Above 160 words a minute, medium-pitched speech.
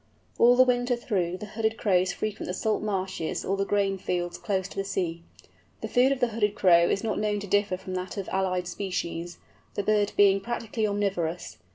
No: average, 200 wpm; high, 195 Hz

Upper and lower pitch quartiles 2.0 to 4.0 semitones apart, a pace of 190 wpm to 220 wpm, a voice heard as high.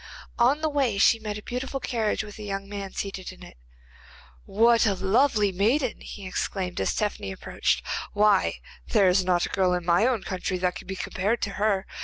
Yes: average, 3.2 semitones; average, 200 wpm; high, 205 Hz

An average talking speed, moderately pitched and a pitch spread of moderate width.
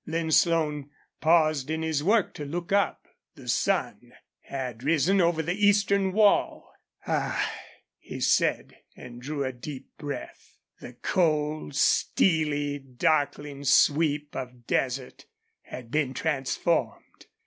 No: slow, 120 wpm; medium, 150 Hz; average, 3.3 semitones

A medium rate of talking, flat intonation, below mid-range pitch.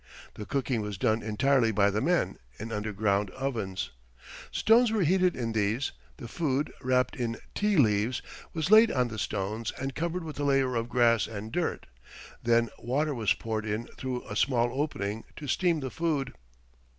No: average, 175 wpm; average, 4.8 semitones; low, 120 Hz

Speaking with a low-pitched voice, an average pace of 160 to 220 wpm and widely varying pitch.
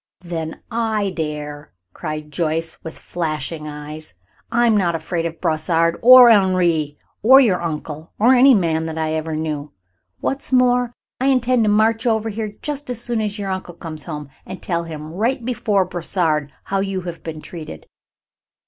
No: medium, 175 Hz; average, 170 wpm; wide, 6.0 semitones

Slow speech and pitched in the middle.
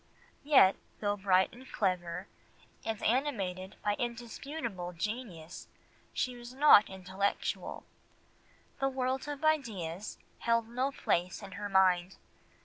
No: slow, 115 wpm; high, 210 Hz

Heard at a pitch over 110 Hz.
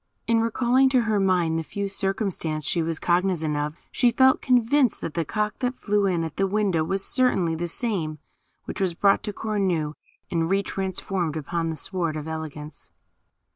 Yes: high, 190 Hz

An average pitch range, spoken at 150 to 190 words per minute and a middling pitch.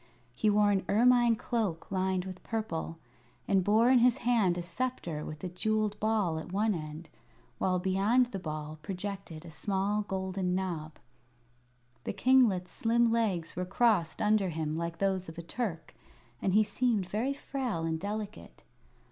No: average, 4.2 semitones; average, 160 wpm; high, 195 Hz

